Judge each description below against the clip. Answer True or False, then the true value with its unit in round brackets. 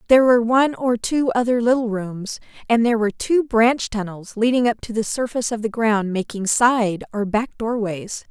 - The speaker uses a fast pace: False (195 wpm)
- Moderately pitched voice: False (225 Hz)